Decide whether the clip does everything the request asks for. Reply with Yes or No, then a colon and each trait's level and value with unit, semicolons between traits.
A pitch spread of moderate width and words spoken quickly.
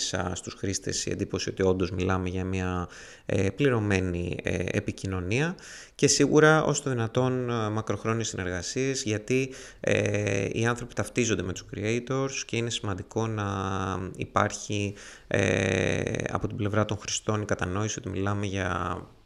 No: average, 4.0 semitones; average, 135 wpm